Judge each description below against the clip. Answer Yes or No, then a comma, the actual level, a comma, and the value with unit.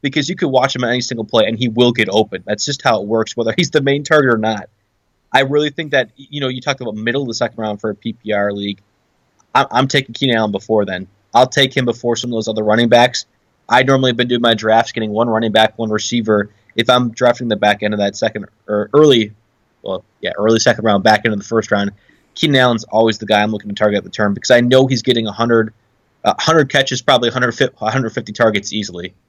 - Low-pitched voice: Yes, low, 115 Hz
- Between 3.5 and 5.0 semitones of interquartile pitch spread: No, average, 2.9 semitones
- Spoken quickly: Yes, fast, 245 wpm